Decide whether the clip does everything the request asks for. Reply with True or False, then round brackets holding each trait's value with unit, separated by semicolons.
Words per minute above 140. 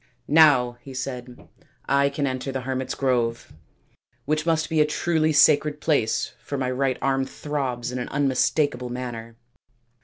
True (175 wpm)